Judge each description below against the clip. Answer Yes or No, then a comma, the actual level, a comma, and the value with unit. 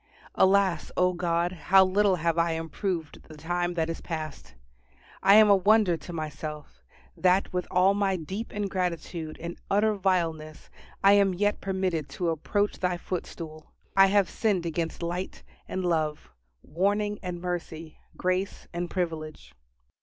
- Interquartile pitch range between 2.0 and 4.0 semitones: Yes, average, 2.9 semitones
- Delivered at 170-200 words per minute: No, average, 145 wpm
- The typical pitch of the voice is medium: Yes, medium, 180 Hz